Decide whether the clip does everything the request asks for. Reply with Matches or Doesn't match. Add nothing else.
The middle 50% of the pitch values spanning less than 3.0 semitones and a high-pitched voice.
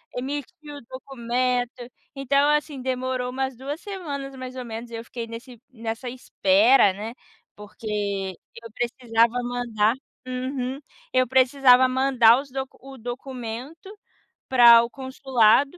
Matches